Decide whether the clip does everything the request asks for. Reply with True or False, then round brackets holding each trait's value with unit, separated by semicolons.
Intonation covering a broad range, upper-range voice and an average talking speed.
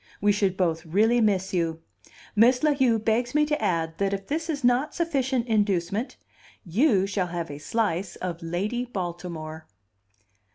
True (5.9 semitones; 200 Hz; 160 wpm)